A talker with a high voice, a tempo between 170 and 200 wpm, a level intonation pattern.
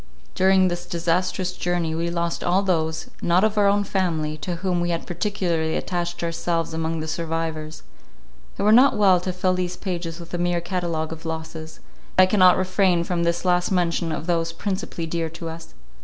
No: medium, 175 Hz; average, 190 wpm; narrow, 1.9 semitones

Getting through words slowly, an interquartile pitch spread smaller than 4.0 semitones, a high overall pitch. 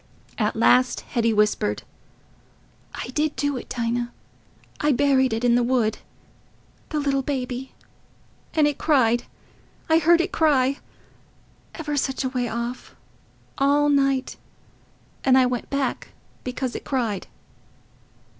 Yes: slow, 125 wpm; average, 2.9 semitones; very high, 260 Hz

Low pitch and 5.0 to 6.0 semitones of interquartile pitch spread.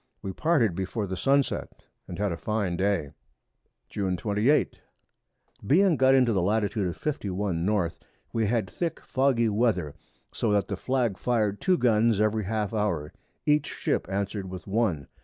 No: low, 105 Hz; average, 3.9 semitones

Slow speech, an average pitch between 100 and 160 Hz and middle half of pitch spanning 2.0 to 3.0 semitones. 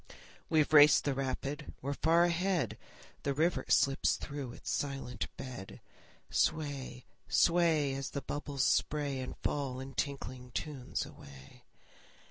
Yes: slow, 125 wpm; medium, 140 Hz; narrow, 2.5 semitones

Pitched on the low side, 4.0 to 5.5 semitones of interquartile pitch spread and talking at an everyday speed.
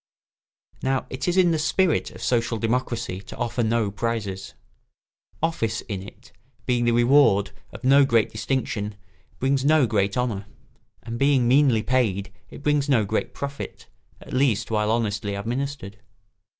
Yes: low, 120 Hz; average, 4.3 semitones; average, 150 wpm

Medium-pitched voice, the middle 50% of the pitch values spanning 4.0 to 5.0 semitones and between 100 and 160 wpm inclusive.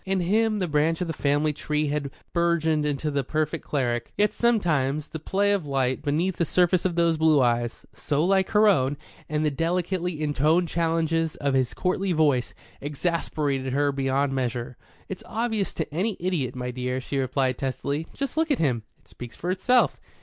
No: medium, 155 Hz; average, 4.5 semitones; average, 185 wpm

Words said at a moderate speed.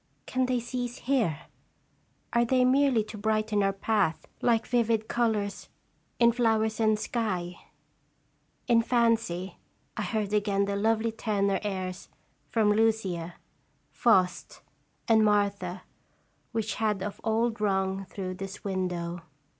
No: slow, 125 wpm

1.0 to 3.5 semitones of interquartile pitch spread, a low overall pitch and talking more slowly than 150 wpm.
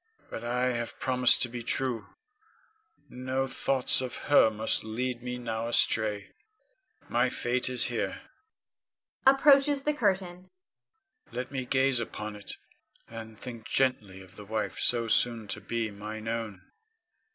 Yes: average, 2.8 semitones; low, 120 Hz; average, 140 wpm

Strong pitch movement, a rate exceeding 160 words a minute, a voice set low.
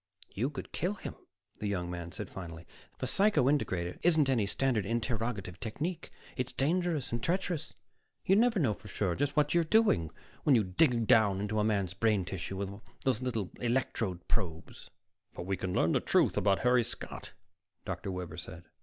Yes: wide, 6.7 semitones; average, 180 wpm; low, 110 Hz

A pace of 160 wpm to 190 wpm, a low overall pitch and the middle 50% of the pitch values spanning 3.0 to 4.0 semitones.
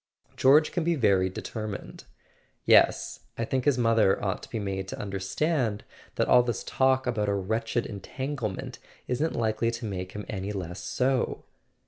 No: average, 175 wpm; low, 115 Hz; average, 4.6 semitones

